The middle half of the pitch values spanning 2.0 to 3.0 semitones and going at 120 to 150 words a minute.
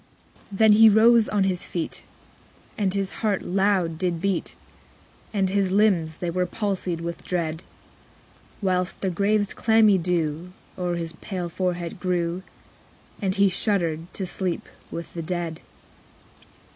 Yes: average, 2.7 semitones; average, 145 wpm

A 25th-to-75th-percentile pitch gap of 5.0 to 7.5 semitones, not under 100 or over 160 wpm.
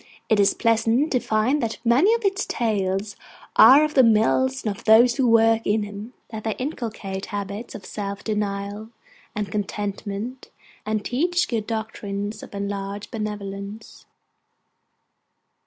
No: average, 2.8 semitones; average, 140 wpm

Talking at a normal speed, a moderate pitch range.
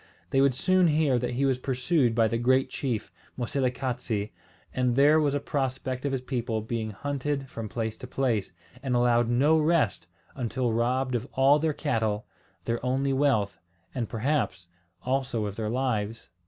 Yes: average, 170 wpm; average, 3.0 semitones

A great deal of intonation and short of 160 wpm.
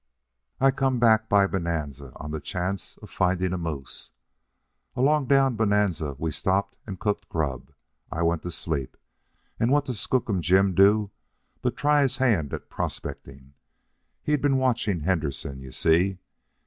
Yes: wide, 6.6 semitones; average, 150 wpm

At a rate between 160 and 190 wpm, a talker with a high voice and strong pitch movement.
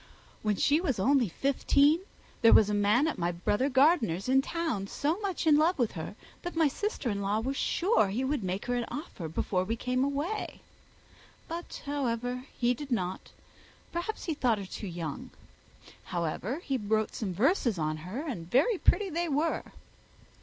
Yes: average, 180 wpm; very high, 250 Hz; wide, 6.9 semitones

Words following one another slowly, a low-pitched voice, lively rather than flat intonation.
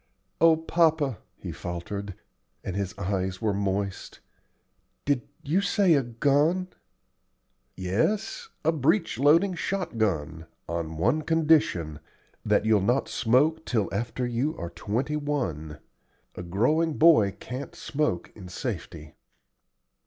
Yes: slow, 120 wpm; low, 120 Hz; wide, 8.6 semitones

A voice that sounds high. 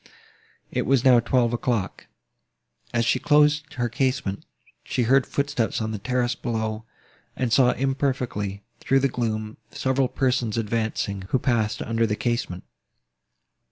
No: low, 120 Hz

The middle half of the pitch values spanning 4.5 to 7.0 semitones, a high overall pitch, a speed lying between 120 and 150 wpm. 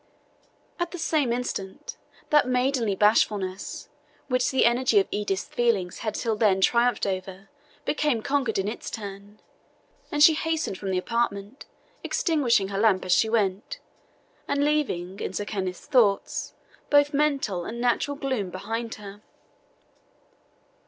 Yes: average, 5.1 semitones; high, 225 Hz; average, 140 wpm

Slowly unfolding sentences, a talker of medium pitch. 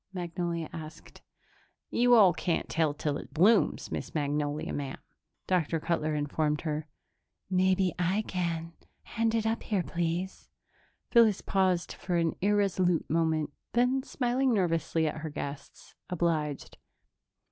Yes: slow, 125 wpm; medium, 170 Hz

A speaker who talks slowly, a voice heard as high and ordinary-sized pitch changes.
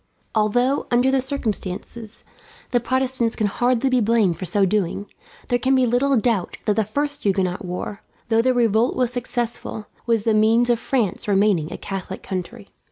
No: average, 170 wpm; high, 230 Hz; average, 3.4 semitones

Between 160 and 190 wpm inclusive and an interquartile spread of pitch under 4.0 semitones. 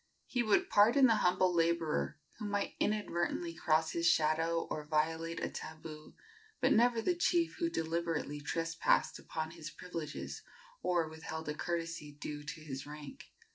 No: average, 150 wpm; average, 2.9 semitones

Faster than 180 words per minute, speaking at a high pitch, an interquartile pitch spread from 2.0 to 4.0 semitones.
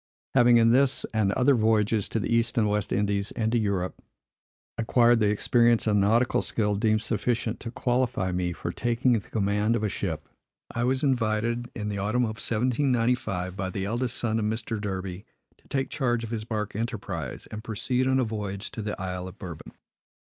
No: average, 190 wpm; low, 110 Hz; average, 2.8 semitones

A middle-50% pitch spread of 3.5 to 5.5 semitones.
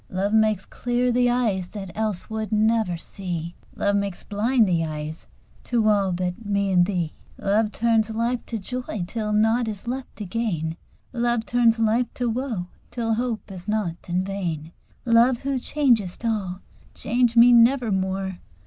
Yes: average, 3.9 semitones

